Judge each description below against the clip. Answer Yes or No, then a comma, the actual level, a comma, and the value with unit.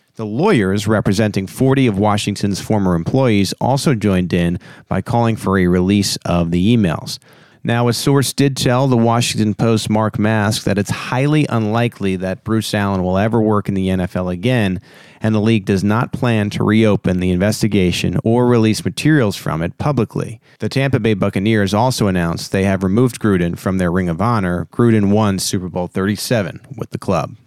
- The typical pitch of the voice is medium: No, low, 105 Hz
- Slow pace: No, average, 180 wpm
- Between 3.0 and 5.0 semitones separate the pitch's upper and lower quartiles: Yes, average, 3.7 semitones